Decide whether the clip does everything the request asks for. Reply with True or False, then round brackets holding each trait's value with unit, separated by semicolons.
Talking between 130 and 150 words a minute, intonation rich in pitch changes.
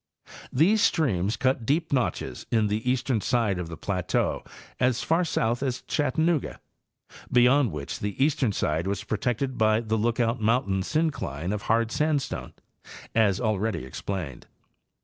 False (145 wpm; 4.7 semitones)